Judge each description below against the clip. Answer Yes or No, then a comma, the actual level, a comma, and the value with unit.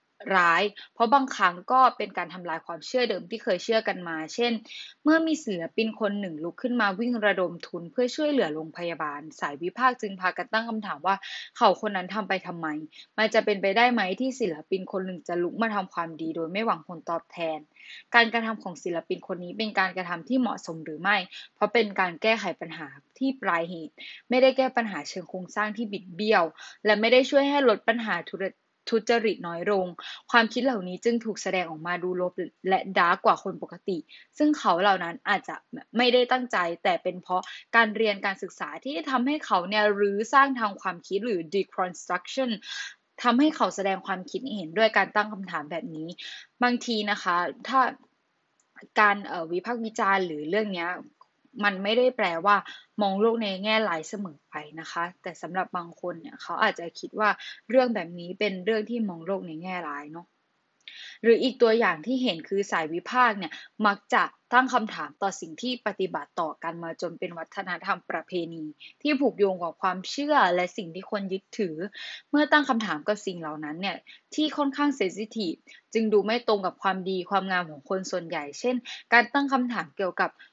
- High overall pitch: Yes, high, 205 Hz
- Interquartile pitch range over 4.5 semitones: Yes, average, 5.0 semitones